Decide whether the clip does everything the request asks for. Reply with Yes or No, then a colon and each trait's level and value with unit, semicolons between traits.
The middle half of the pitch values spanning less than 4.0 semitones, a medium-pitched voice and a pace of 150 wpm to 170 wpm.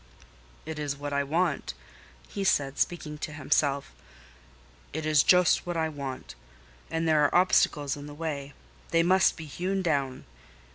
Yes: average, 2.8 semitones; medium, 150 Hz; average, 155 wpm